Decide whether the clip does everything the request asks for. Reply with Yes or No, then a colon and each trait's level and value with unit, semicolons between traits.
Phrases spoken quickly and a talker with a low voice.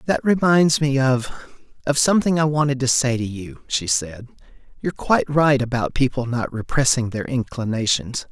No: average, 160 wpm; low, 130 Hz